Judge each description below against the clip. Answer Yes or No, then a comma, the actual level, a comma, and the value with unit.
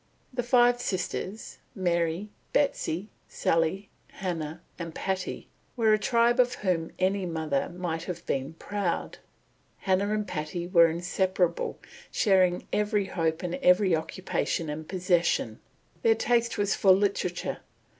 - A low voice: No, medium, 185 Hz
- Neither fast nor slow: No, slow, 125 wpm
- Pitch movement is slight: No, average, 3.6 semitones